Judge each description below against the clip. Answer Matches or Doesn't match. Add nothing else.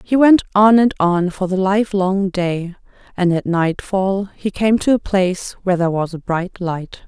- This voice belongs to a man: Doesn't match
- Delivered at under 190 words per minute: Doesn't match